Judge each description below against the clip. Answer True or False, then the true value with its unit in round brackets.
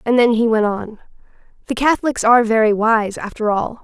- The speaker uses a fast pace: False (190 wpm)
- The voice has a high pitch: True (225 Hz)